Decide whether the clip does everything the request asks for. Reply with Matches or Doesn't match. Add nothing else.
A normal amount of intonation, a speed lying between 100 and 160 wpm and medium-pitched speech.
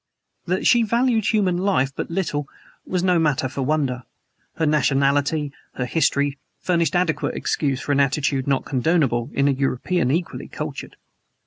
Matches